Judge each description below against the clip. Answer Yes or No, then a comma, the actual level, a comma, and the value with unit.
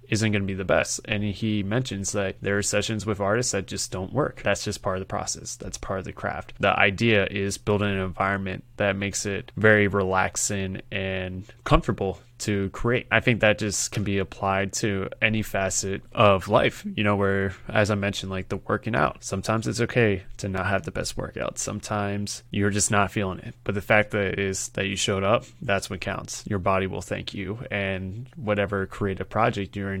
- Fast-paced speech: Yes, fast, 210 wpm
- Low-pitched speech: Yes, low, 100 Hz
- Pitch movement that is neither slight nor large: No, narrow, 2.0 semitones